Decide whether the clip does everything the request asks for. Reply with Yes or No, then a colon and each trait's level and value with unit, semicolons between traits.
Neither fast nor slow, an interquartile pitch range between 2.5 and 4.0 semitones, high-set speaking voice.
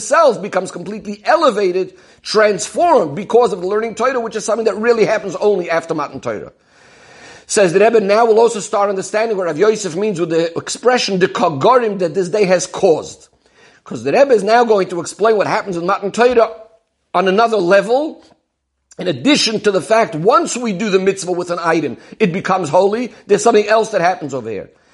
Yes: average, 190 wpm; average, 3.2 semitones; high, 210 Hz